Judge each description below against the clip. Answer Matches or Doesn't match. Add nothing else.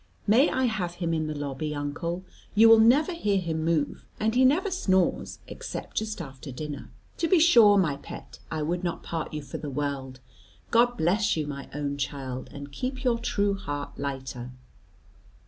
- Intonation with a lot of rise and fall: Matches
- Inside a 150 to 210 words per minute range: Matches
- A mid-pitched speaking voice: Matches